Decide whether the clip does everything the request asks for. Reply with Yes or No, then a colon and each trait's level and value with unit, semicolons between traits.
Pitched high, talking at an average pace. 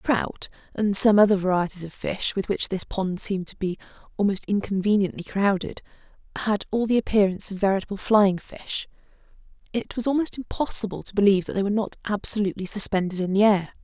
Yes: high, 200 Hz; average, 180 wpm